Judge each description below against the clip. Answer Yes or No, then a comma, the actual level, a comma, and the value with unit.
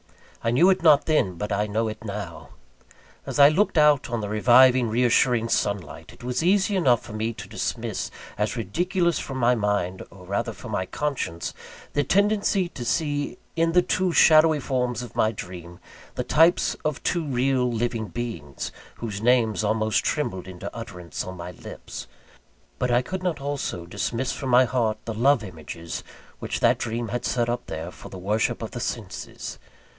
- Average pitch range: No, wide, 5.8 semitones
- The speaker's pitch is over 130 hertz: No, low, 120 Hz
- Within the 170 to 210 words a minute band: Yes, average, 180 wpm